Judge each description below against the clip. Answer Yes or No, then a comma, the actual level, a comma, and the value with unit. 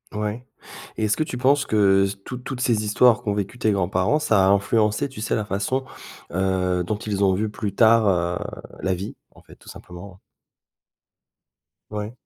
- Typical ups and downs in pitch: Yes, average, 3.1 semitones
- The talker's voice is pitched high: No, low, 105 Hz